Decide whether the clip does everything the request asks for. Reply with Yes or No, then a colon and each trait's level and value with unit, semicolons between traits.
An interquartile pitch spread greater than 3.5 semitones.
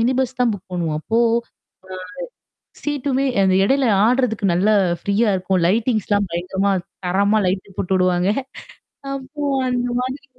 Yes: average, 5.1 semitones